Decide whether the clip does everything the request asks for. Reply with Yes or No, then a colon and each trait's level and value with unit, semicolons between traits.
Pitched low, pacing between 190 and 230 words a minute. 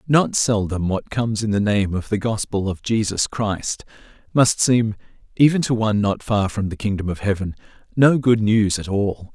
Yes: low, 105 Hz; average, 195 wpm